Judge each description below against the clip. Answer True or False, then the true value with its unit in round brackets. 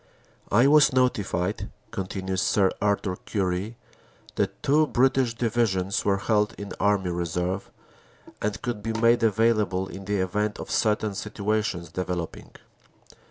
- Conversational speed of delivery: False (125 wpm)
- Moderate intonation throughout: True (3.2 semitones)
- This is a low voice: True (105 Hz)